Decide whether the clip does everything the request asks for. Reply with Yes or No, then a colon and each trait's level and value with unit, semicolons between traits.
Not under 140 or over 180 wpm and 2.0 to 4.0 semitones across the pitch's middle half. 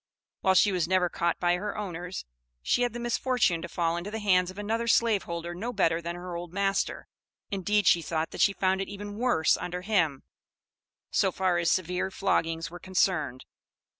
No: average, 190 wpm; average, 3.1 semitones